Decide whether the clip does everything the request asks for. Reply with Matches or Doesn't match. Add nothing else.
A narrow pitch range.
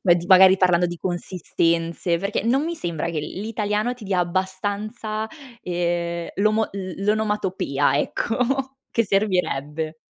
Doesn't match